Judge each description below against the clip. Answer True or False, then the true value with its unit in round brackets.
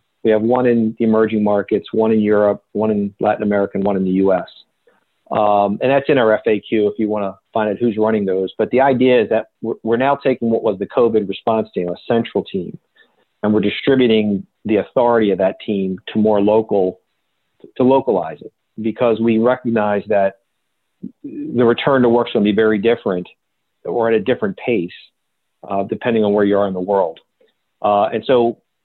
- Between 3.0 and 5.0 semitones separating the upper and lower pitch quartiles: False (2.5 semitones)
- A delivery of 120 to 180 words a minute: False (200 wpm)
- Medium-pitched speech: False (110 Hz)